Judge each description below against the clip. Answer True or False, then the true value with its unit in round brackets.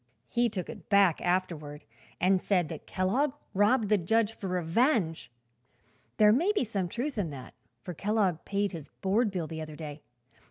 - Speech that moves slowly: False (170 wpm)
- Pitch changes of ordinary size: True (4.8 semitones)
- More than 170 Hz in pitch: True (190 Hz)